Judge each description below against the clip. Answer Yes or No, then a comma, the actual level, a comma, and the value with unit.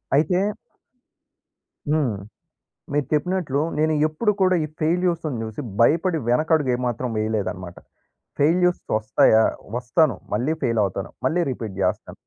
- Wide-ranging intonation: Yes, wide, 6.4 semitones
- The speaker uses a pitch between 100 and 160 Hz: Yes, medium, 145 Hz